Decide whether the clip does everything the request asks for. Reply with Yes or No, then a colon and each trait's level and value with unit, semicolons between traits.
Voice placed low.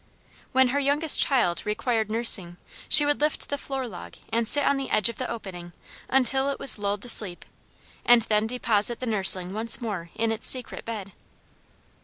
No: high, 230 Hz